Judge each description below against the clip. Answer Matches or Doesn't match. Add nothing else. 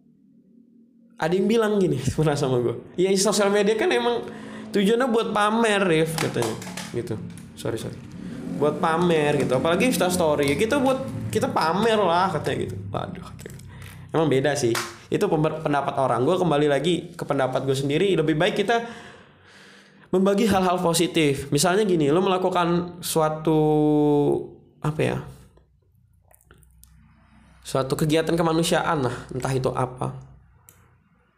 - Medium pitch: Matches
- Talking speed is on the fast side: Doesn't match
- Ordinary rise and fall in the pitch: Doesn't match